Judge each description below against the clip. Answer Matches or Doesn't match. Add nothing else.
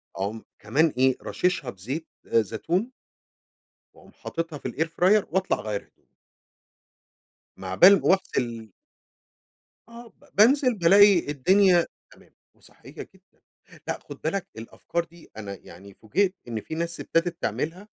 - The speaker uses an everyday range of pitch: Doesn't match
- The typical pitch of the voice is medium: Matches